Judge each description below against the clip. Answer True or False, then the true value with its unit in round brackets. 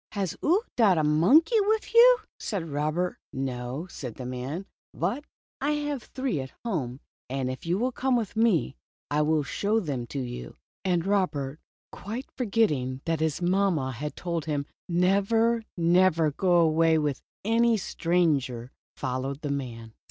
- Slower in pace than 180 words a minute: True (160 wpm)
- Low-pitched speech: False (165 Hz)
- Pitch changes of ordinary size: False (6.9 semitones)